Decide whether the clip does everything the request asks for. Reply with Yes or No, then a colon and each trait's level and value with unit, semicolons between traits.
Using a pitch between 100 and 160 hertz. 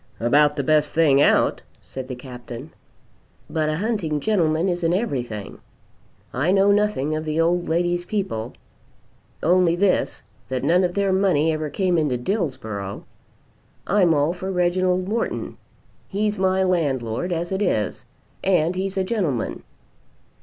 No: medium, 170 Hz